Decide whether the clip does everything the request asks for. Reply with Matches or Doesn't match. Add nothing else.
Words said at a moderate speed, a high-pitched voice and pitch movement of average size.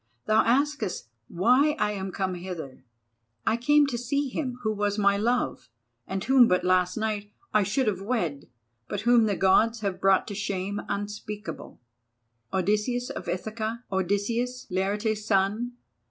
Matches